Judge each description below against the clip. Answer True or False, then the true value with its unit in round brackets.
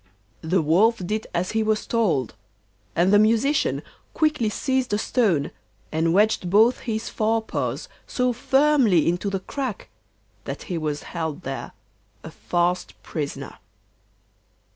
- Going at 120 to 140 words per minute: True (135 wpm)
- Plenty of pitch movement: False (5.0 semitones)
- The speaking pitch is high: True (205 Hz)